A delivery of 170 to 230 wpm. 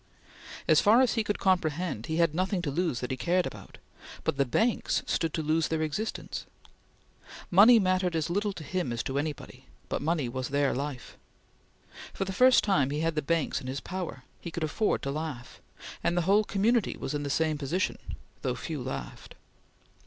Yes: average, 195 wpm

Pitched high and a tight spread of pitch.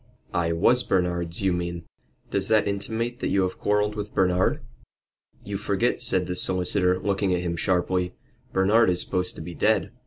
No: very low, 95 Hz; narrow, 2.3 semitones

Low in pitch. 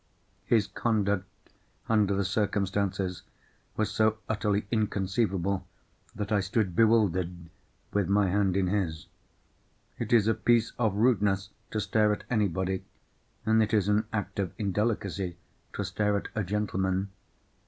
Yes: low, 100 Hz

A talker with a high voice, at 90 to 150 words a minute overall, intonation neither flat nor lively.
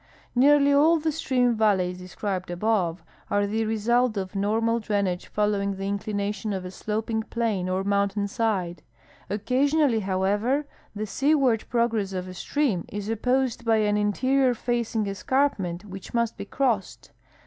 Yes: high, 215 Hz; average, 145 wpm; average, 3.5 semitones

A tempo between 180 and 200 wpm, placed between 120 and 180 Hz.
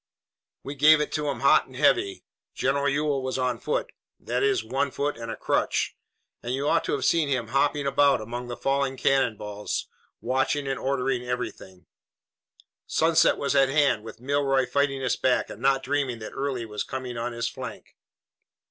Yes: average, 185 wpm; low, 135 Hz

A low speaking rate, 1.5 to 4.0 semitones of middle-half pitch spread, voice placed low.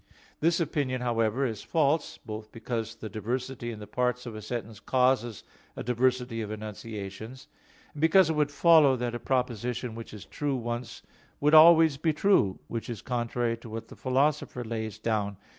No: average, 175 wpm; average, 3.3 semitones; low, 120 Hz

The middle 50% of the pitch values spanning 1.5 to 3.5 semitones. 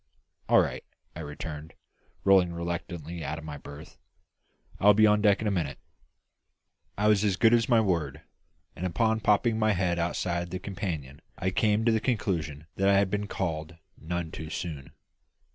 No: average, 4.5 semitones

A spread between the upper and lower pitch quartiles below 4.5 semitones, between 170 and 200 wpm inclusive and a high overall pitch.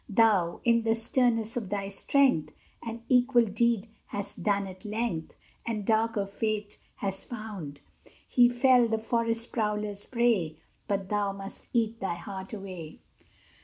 No: average, 2.9 semitones; average, 140 wpm; high, 215 Hz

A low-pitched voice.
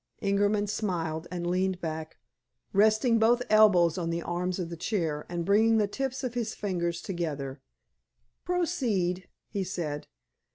No: medium, 185 Hz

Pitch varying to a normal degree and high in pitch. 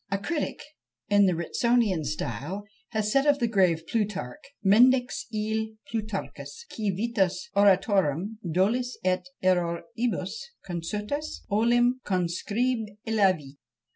Yes: average, 4.2 semitones; high, 205 Hz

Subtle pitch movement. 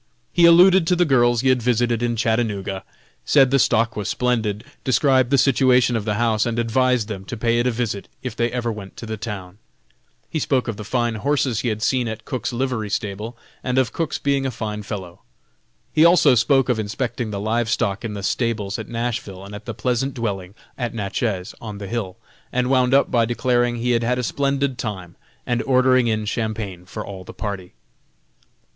No: average, 3.2 semitones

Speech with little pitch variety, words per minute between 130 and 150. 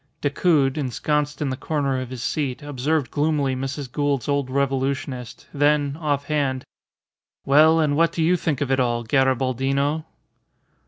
Yes: narrow, 2.1 semitones; average, 145 wpm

